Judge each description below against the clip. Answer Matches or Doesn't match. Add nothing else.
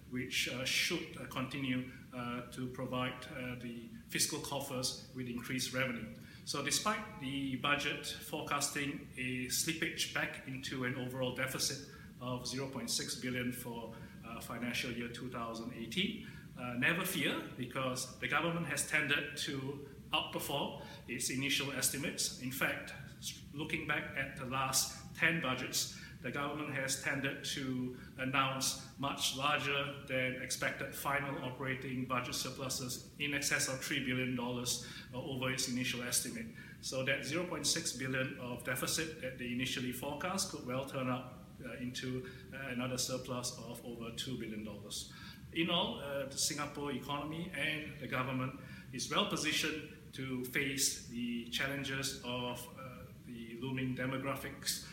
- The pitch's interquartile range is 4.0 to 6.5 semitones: Doesn't match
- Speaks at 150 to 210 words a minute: Doesn't match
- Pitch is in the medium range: Doesn't match